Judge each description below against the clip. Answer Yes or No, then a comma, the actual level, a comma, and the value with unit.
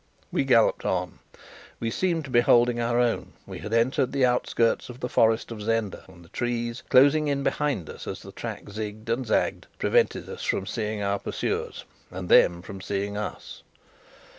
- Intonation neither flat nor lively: Yes, average, 3.3 semitones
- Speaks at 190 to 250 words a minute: No, average, 180 wpm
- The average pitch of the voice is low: Yes, low, 115 Hz